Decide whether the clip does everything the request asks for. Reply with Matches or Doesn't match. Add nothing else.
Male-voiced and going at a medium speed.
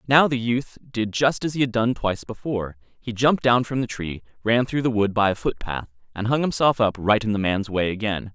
Doesn't match